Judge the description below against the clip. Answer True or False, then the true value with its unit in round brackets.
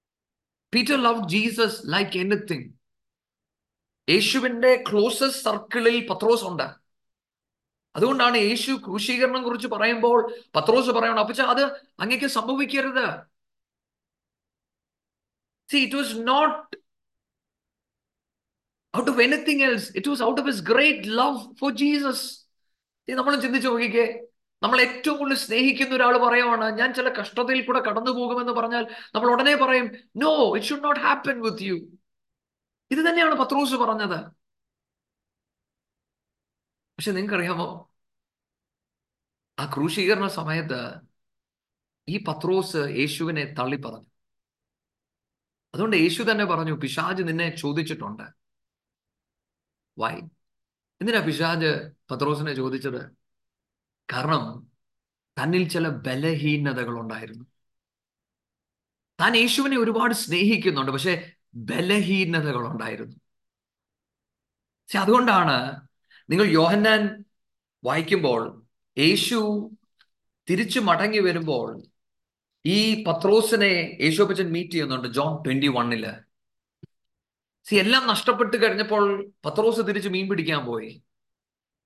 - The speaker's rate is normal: False (90 wpm)